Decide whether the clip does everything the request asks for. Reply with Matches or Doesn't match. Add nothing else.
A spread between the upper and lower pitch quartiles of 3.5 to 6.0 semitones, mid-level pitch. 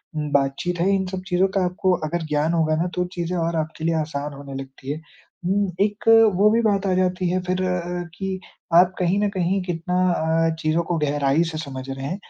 Doesn't match